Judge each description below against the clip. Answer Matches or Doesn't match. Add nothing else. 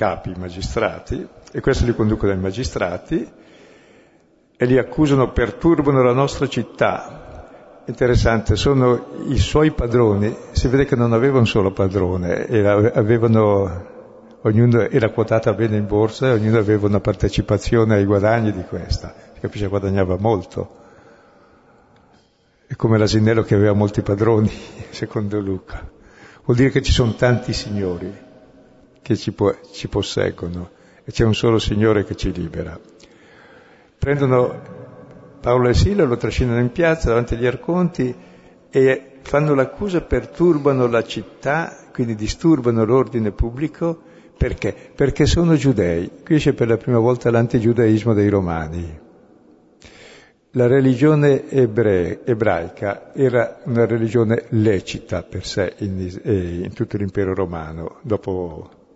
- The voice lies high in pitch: Doesn't match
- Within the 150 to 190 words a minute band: Doesn't match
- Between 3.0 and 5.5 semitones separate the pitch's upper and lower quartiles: Matches